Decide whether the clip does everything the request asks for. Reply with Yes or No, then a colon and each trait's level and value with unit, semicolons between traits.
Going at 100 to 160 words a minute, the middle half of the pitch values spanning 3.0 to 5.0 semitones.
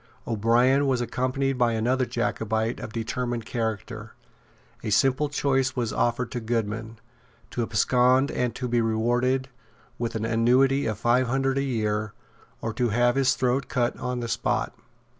No: average, 155 wpm; narrow, 2.4 semitones